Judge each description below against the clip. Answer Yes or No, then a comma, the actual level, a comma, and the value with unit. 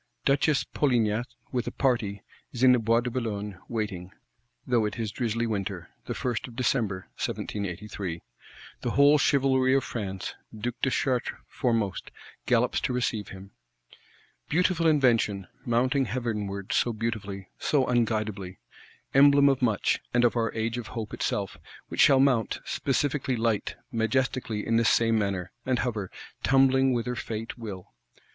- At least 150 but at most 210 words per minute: No, average, 140 wpm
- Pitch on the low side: Yes, low, 115 Hz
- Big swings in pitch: No, average, 3.7 semitones